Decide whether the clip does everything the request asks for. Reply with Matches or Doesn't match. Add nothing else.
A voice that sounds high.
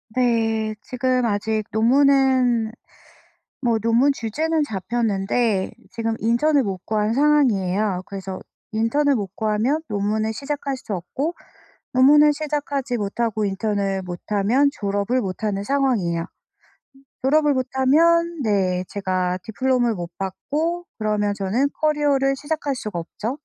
Matches